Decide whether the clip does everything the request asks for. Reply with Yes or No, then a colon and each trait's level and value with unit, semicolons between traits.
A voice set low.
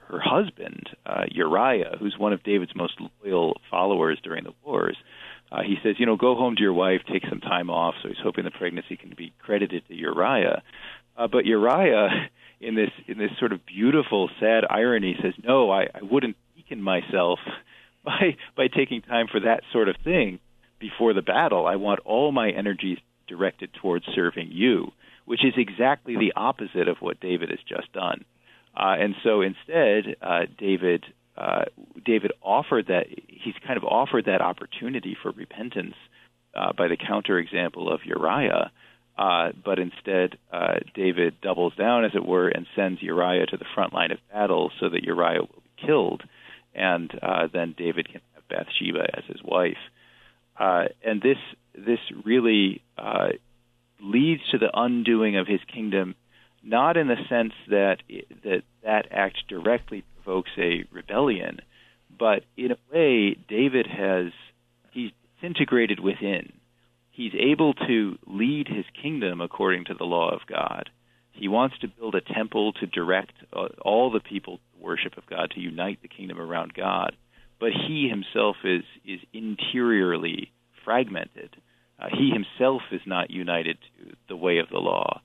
Yes: low, 100 Hz